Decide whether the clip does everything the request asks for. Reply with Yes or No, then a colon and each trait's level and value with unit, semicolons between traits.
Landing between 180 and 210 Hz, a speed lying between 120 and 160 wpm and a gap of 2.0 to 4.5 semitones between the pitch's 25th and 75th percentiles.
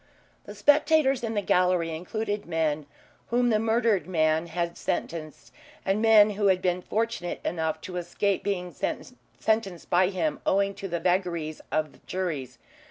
Yes: medium, 185 Hz; average, 150 wpm; average, 4.1 semitones